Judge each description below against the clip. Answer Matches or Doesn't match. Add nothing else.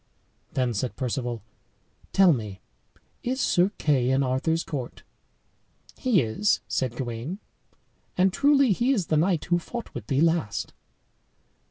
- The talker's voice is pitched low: Doesn't match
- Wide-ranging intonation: Matches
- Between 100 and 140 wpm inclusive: Matches